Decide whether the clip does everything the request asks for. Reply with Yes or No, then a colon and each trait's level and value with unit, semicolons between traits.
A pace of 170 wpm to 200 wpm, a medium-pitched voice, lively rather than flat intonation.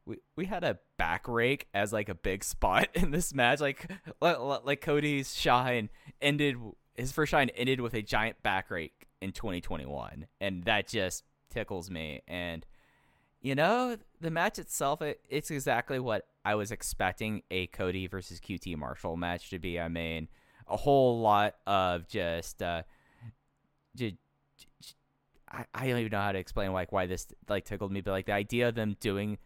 No: average, 180 wpm; low, 105 Hz; wide, 6.9 semitones